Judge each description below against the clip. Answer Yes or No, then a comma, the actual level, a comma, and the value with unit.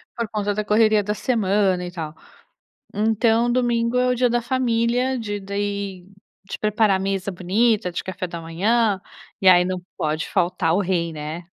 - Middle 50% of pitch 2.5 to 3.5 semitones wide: No, average, 4.1 semitones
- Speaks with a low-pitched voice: No, high, 205 Hz